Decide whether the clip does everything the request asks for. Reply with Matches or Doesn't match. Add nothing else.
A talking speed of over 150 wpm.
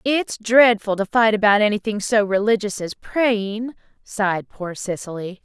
Doesn't match